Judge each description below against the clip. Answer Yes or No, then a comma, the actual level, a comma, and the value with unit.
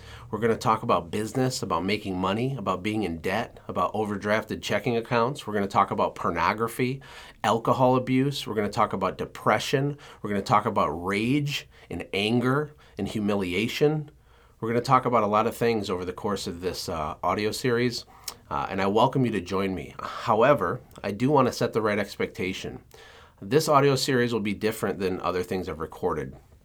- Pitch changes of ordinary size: Yes, average, 3.7 semitones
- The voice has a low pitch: Yes, low, 115 Hz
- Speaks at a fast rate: No, average, 195 wpm